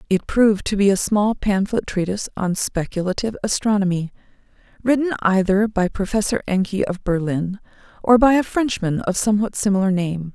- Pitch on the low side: No, high, 200 Hz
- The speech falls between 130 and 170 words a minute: Yes, average, 150 wpm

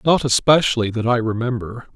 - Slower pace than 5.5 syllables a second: No, 5.7 syllables/s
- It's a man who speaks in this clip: Yes, male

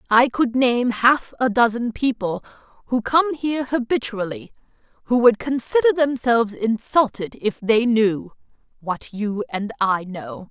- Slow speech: Yes, slow, 130 wpm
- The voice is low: No, high, 235 Hz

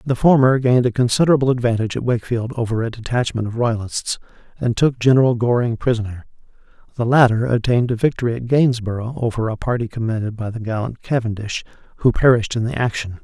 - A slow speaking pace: No, average, 170 wpm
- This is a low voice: Yes, low, 120 Hz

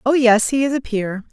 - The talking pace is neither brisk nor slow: No, fast, 275 wpm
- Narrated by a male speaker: No, female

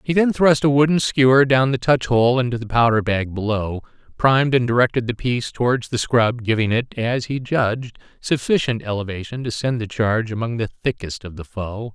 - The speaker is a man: Yes, male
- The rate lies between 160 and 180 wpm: No, average, 200 wpm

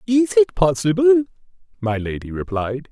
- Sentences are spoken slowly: Yes, slow, 125 wpm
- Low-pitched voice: No, medium, 175 Hz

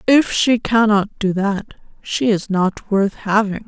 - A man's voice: No, female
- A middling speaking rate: Yes, average, 165 wpm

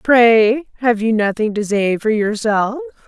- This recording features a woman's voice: Yes, female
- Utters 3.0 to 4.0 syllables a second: Yes, 3.8 syllables/s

